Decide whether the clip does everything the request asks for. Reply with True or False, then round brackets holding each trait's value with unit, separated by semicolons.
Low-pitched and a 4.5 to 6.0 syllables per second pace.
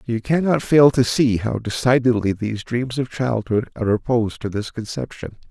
True (120 Hz; 5.2 syllables/s)